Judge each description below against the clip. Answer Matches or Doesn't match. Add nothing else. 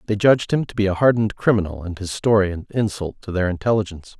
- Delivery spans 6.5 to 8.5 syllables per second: Matches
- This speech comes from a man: Matches